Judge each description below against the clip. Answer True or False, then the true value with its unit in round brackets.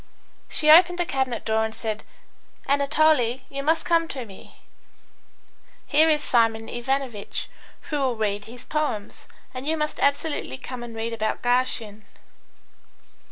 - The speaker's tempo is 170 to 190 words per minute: False (140 wpm)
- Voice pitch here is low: False (255 Hz)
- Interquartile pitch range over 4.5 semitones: True (5.2 semitones)